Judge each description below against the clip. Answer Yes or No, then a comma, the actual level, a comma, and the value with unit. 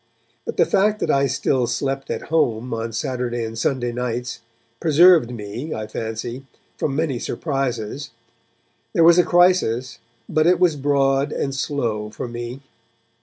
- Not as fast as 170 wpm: Yes, average, 150 wpm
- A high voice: No, low, 135 Hz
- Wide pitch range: No, average, 4.1 semitones